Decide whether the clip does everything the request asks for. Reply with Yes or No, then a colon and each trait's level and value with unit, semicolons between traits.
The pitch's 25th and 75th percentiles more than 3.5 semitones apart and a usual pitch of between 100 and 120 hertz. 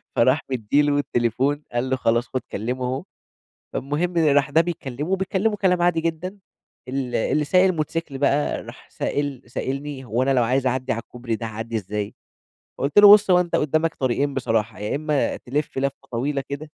No: average, 4.2 semitones; medium, 140 Hz